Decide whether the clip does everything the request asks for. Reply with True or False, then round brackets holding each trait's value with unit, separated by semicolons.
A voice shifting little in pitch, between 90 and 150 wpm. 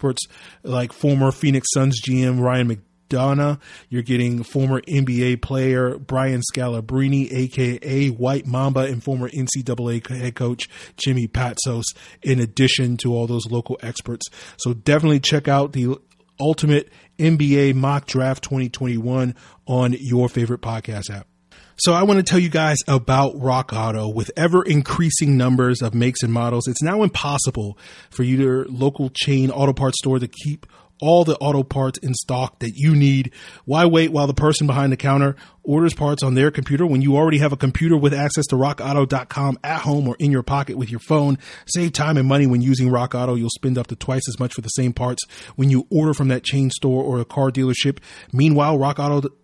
False (2.3 semitones; 180 wpm)